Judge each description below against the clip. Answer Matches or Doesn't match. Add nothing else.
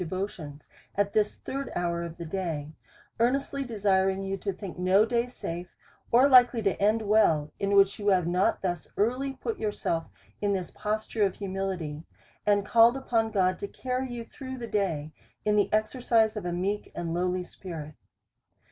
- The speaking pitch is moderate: Doesn't match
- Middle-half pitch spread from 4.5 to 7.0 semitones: Doesn't match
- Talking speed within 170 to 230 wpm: Matches